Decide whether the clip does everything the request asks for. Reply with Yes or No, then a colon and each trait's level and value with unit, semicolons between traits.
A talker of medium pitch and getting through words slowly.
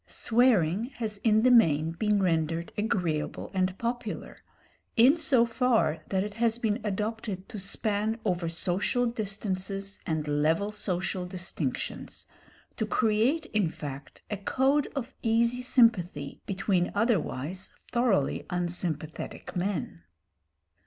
No: high, 200 Hz; slow, 120 wpm